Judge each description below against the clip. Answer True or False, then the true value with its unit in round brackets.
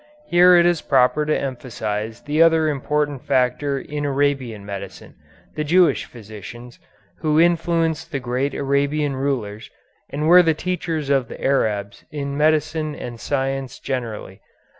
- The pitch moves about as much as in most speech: True (3.7 semitones)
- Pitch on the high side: False (140 Hz)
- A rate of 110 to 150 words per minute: True (140 wpm)